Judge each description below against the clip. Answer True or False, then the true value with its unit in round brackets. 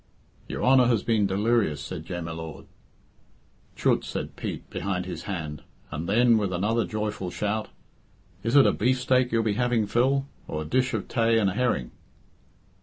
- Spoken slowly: False (175 wpm)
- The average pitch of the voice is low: True (105 Hz)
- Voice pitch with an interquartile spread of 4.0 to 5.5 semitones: True (4.9 semitones)